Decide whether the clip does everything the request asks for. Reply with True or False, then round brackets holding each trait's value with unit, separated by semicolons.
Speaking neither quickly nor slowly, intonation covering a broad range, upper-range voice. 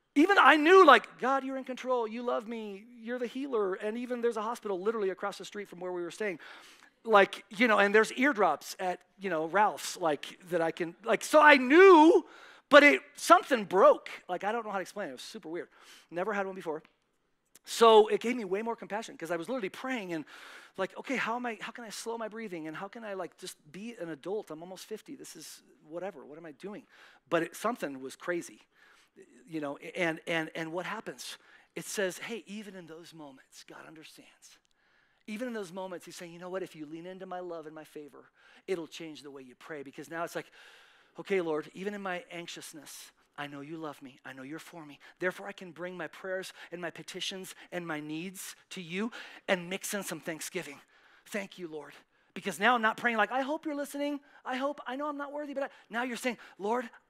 False (230 wpm; 5.7 semitones; 195 Hz)